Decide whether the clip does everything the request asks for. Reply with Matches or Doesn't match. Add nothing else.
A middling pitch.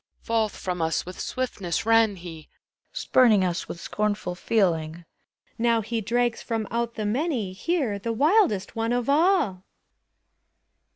Doesn't match